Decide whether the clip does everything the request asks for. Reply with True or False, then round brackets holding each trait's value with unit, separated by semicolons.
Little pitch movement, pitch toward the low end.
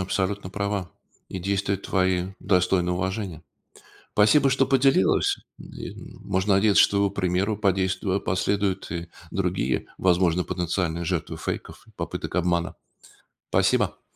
True (2.0 semitones; 95 Hz)